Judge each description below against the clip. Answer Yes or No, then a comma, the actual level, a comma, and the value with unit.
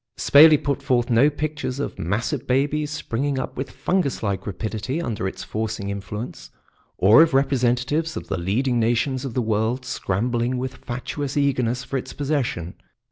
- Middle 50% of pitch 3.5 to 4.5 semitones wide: Yes, average, 3.9 semitones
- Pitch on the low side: Yes, low, 125 Hz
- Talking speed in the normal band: Yes, average, 160 wpm